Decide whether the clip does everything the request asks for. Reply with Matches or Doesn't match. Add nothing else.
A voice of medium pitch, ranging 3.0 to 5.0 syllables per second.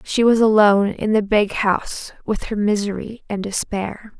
Doesn't match